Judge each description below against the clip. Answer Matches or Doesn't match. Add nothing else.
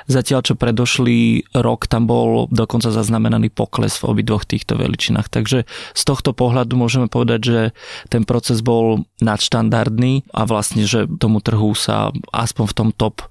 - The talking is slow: Doesn't match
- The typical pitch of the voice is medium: Doesn't match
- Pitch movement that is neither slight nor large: Doesn't match